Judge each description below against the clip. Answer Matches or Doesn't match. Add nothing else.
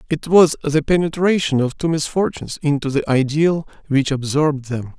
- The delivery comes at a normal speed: Matches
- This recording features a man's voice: Matches